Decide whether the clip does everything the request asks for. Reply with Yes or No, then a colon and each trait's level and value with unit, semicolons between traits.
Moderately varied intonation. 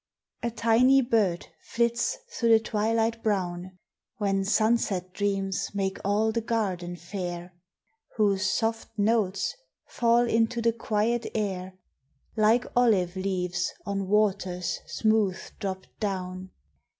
Yes: average, 3.3 semitones